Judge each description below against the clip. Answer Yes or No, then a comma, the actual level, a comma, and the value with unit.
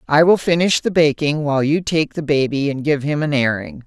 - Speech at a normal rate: No, fast, 235 wpm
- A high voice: No, medium, 150 Hz